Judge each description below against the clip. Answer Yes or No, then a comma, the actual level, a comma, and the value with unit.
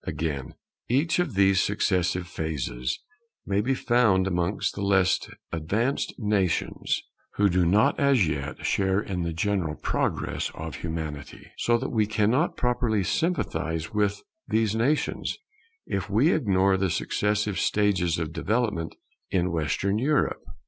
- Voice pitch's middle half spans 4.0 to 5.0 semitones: Yes, average, 4.5 semitones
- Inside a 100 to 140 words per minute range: Yes, slow, 135 wpm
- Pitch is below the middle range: Yes, low, 100 Hz